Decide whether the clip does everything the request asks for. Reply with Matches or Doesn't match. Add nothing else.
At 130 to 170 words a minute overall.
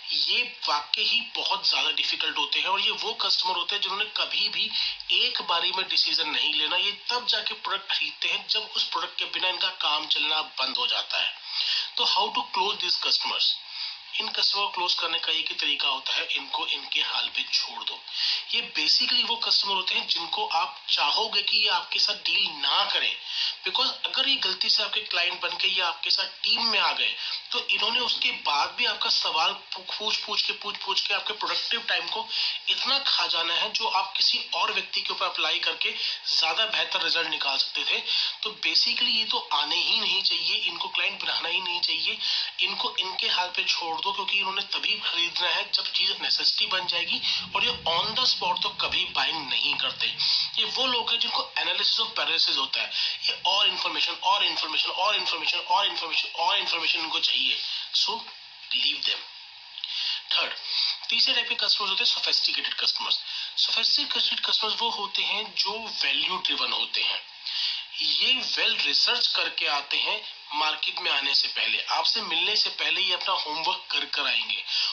Doesn't match